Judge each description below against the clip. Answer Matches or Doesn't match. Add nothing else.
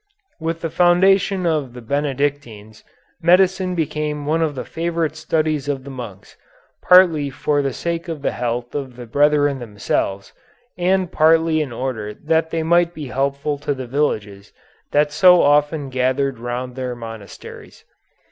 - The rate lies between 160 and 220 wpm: Doesn't match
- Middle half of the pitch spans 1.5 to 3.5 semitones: Doesn't match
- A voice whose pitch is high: Doesn't match